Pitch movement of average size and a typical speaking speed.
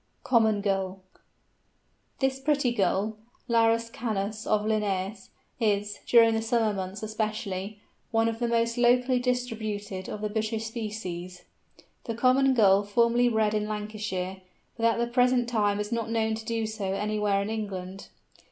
No: narrow, 2.2 semitones; average, 150 wpm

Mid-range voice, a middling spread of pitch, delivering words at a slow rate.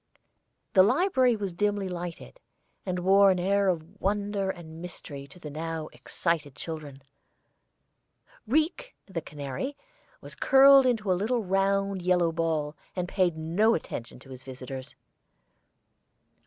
Yes: medium, 180 Hz; average, 4.2 semitones; slow, 130 wpm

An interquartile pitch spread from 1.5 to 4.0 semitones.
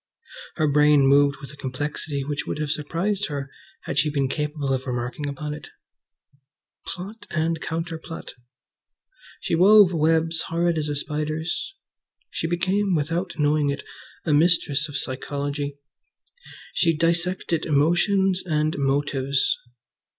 Yes: average, 2.8 semitones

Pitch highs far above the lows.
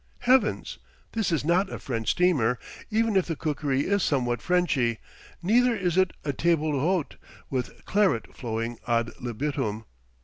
Yes: wide, 7.3 semitones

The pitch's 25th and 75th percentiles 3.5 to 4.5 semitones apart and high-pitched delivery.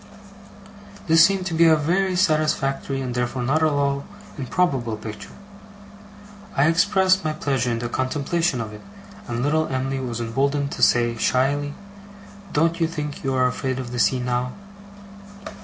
No: average, 4.1 semitones; medium, 140 Hz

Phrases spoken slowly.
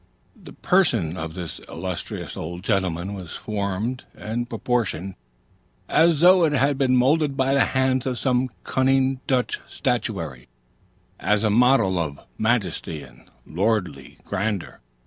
Yes: slow, 130 wpm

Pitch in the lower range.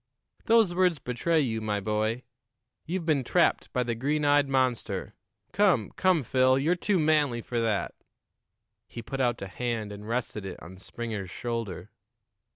Yes: low, 125 Hz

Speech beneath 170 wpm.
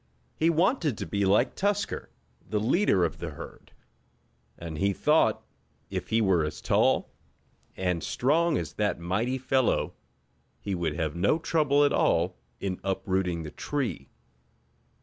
Yes: average, 145 wpm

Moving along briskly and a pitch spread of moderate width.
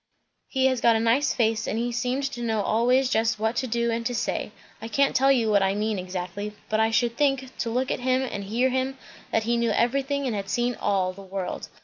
Yes: fast, 245 wpm; average, 3.1 semitones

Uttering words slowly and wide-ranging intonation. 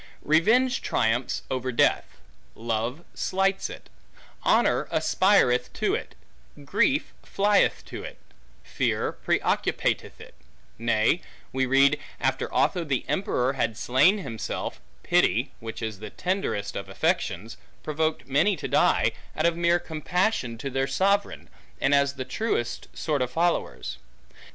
Yes: slow, 130 wpm; wide, 6.8 semitones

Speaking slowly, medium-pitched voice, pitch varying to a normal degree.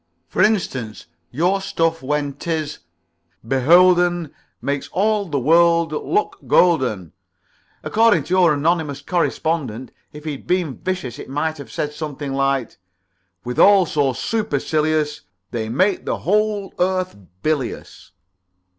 Yes: slow, 125 wpm; medium, 155 Hz; average, 4.8 semitones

